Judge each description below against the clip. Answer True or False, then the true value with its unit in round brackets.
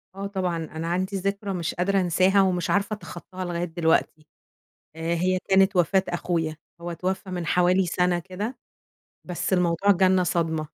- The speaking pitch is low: False (180 Hz)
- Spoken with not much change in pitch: True (2.1 semitones)